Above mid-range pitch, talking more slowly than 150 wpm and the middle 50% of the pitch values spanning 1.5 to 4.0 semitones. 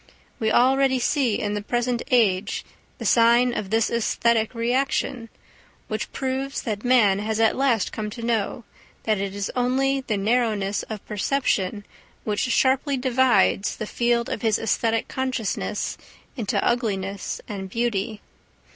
Yes: high, 230 Hz; average, 140 wpm; average, 3.3 semitones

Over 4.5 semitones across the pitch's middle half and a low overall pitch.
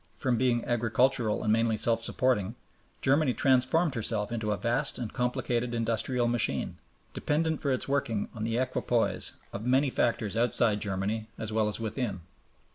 No: average, 2.7 semitones; low, 120 Hz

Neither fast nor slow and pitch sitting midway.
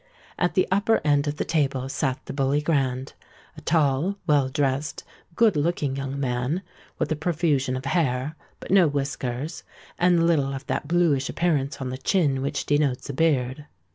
Yes: average, 170 wpm; medium, 145 Hz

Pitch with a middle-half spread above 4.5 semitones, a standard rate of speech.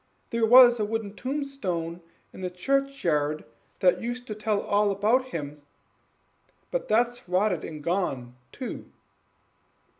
No: wide, 5.6 semitones; slow, 125 wpm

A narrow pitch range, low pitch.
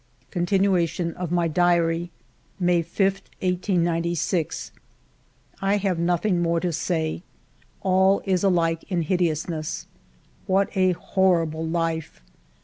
No: narrow, 2.0 semitones; medium, 175 Hz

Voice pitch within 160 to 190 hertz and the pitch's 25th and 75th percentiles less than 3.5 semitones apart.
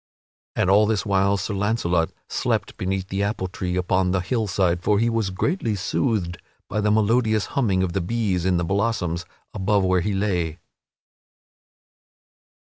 No: very low, 95 Hz; narrow, 2.6 semitones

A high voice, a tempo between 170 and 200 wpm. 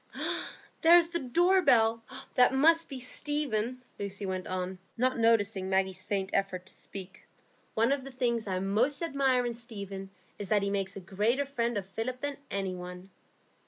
Yes: high, 225 Hz; average, 180 wpm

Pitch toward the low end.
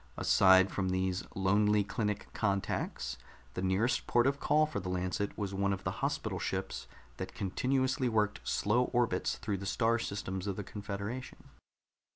Yes: low, 100 Hz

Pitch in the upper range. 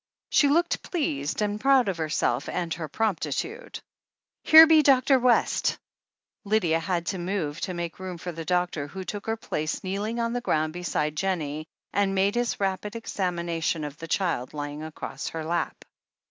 No: medium, 180 Hz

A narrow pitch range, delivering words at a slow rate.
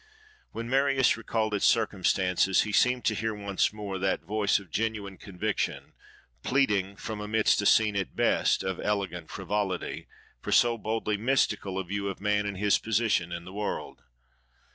No: narrow, 2.3 semitones; average, 165 wpm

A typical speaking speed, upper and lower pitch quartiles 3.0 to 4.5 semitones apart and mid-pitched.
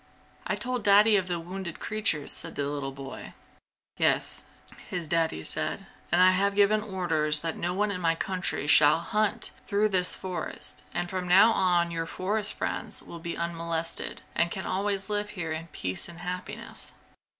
Yes: average, 170 wpm; average, 3.3 semitones; medium, 180 Hz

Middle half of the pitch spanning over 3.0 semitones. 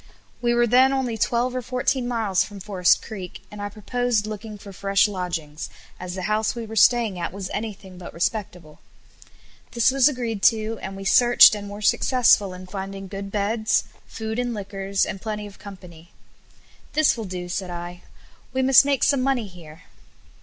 Yes: average, 3.9 semitones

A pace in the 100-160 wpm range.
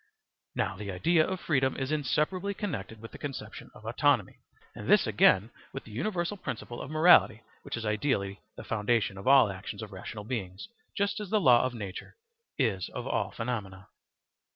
No: average, 175 wpm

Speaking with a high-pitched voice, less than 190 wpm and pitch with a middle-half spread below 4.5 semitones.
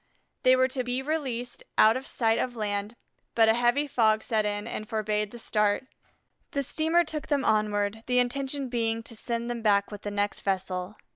No: high, 230 Hz; average, 195 wpm; average, 3.4 semitones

